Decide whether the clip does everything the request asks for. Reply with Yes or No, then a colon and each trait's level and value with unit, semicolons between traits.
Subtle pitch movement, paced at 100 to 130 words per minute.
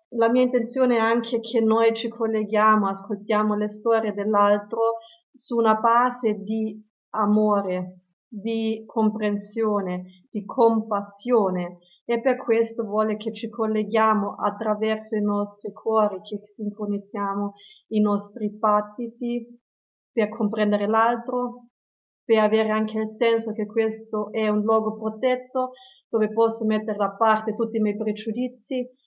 Yes: narrow, 1.5 semitones; average, 125 wpm